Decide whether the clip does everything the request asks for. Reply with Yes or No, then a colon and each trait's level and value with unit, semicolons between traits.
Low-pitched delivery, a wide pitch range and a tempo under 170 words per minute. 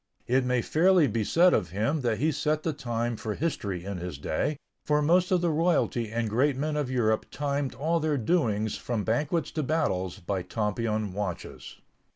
No: low, 125 Hz; wide, 6.3 semitones; average, 190 wpm